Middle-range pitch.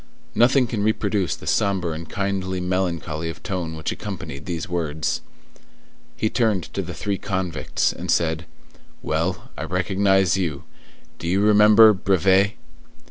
No: very low, 95 Hz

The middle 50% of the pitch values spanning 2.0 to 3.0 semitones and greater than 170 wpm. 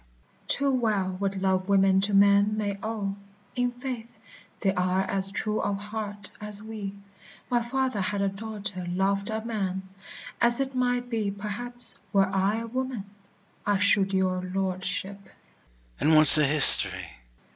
No: narrow, 2.6 semitones; average, 140 wpm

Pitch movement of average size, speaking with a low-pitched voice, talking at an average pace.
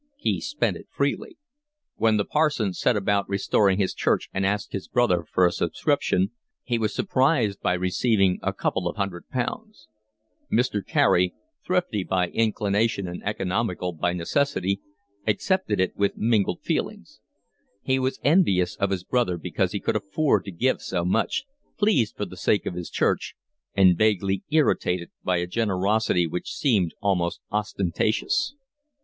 Yes: average, 4.6 semitones; low, 100 Hz; average, 155 wpm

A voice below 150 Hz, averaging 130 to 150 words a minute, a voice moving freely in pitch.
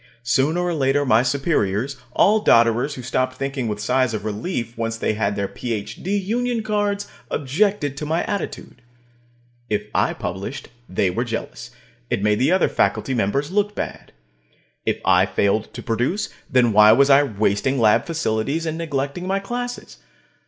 No: low, 135 Hz; average, 160 wpm; wide, 7.2 semitones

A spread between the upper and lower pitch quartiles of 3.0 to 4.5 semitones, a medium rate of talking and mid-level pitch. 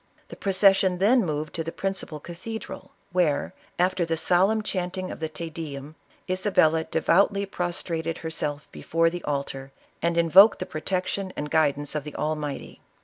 Yes: average, 3.3 semitones; average, 150 wpm; medium, 170 Hz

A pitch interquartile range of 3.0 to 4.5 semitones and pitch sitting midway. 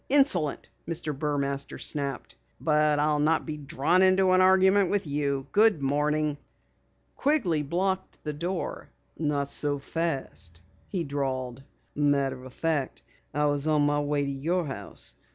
Yes: average, 3.4 semitones; medium, 150 Hz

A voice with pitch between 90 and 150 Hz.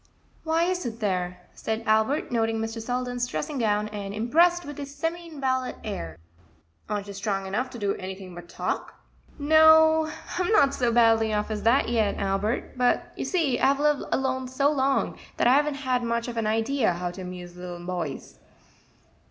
No: high, 235 Hz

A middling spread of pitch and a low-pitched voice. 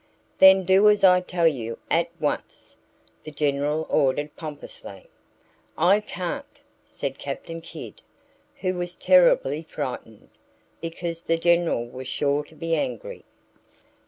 No: average, 3.8 semitones; medium, 165 Hz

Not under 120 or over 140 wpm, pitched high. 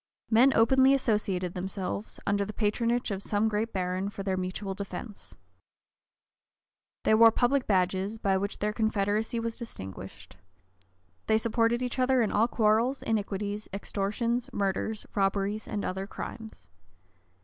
Yes: slow, 135 wpm; high, 210 Hz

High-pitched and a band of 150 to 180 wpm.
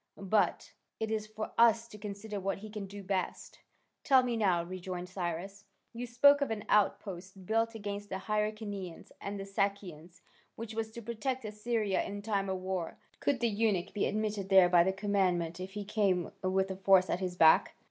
No: high, 200 Hz; average, 190 wpm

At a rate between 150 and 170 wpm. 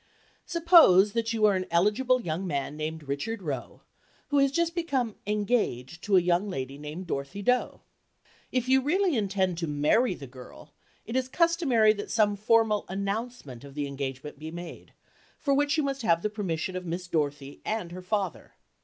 No: average, 180 wpm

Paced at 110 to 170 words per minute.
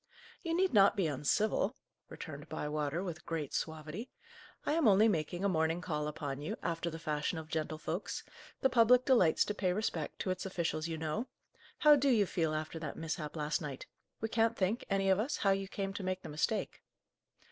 No: average, 195 wpm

